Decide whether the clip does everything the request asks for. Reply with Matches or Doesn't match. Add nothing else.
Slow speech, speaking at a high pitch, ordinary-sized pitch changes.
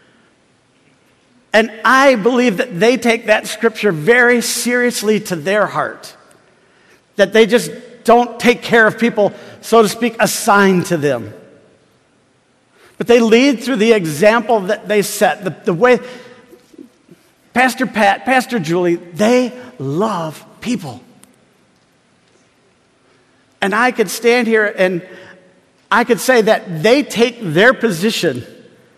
Matches